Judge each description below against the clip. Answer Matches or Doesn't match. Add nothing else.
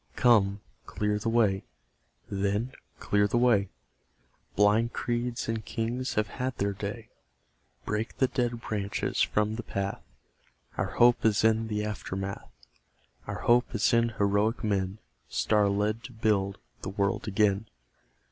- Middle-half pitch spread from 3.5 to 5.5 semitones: Doesn't match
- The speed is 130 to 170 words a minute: Matches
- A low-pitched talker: Matches